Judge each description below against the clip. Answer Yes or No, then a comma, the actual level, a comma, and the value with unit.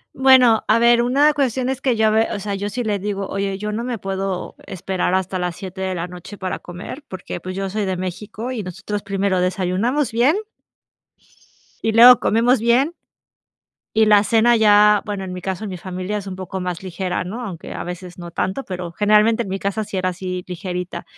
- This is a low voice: No, high, 200 Hz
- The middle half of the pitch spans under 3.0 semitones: No, average, 3.4 semitones